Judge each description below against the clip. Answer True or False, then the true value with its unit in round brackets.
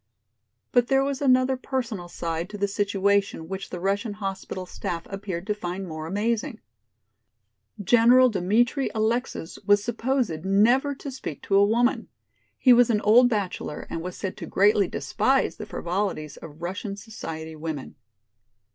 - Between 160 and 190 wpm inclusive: False (150 wpm)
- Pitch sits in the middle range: False (205 Hz)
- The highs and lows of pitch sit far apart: False (4.8 semitones)